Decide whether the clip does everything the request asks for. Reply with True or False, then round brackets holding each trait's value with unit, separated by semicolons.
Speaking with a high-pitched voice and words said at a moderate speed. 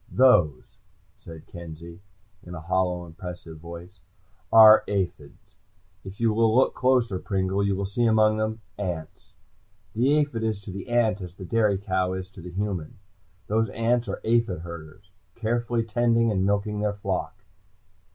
False (100 Hz; 155 wpm)